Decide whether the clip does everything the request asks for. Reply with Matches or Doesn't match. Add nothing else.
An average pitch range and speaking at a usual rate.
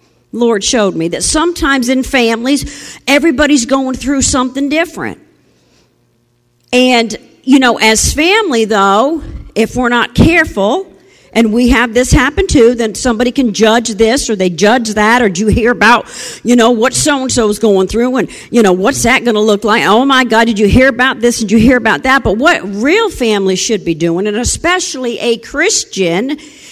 Matches